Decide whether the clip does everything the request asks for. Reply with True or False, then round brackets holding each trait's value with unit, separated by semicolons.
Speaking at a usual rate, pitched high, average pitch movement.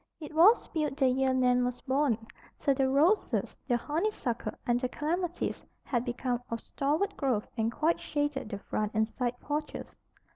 True (170 wpm; 265 Hz; 3.7 semitones)